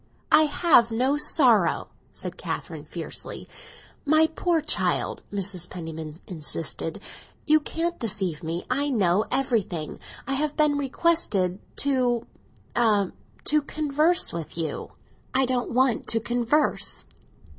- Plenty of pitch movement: Yes, wide, 7.9 semitones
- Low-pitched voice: No, high, 245 Hz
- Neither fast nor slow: No, slow, 115 wpm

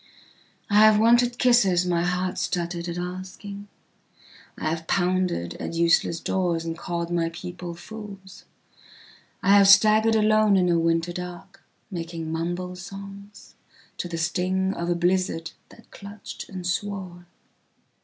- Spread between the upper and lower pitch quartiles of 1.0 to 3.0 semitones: Yes, narrow, 2.5 semitones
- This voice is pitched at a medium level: Yes, medium, 180 Hz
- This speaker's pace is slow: Yes, slow, 125 wpm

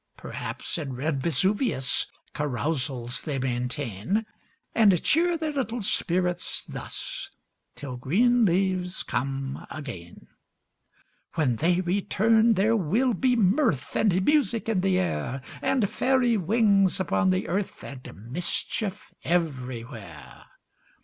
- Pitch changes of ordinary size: No, wide, 8.4 semitones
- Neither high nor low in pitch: Yes, medium, 180 Hz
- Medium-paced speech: No, slow, 110 wpm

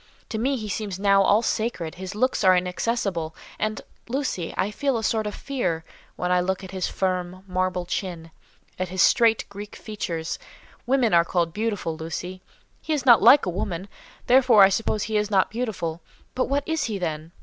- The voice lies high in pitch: Yes, high, 195 Hz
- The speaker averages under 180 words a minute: No, average, 190 wpm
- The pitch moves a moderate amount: Yes, average, 4.0 semitones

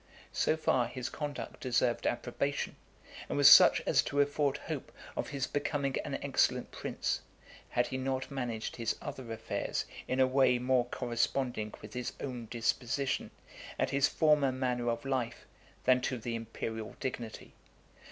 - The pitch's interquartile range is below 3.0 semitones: Yes, narrow, 2.5 semitones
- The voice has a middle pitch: No, low, 130 Hz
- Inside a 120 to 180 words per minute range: Yes, average, 150 wpm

